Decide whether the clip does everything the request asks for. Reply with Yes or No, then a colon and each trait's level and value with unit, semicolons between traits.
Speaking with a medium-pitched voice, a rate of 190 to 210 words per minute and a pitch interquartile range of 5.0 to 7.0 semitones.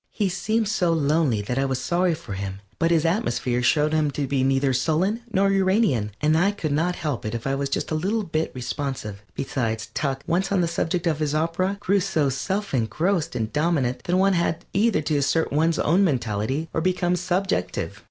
Yes: medium, 160 Hz; fast, 205 wpm; average, 5.3 semitones